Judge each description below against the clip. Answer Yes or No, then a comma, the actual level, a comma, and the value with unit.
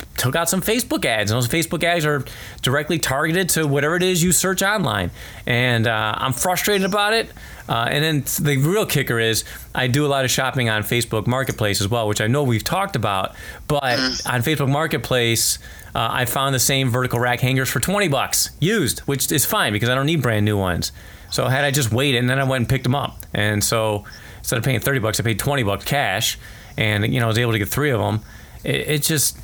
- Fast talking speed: Yes, fast, 230 wpm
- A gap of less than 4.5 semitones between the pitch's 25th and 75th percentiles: No, average, 5.0 semitones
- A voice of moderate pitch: No, low, 130 Hz